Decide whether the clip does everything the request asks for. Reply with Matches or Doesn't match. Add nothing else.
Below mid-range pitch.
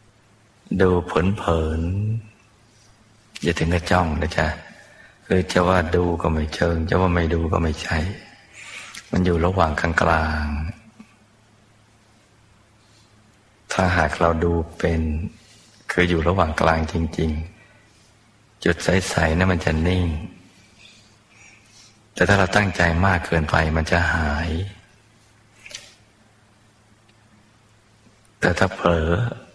Matches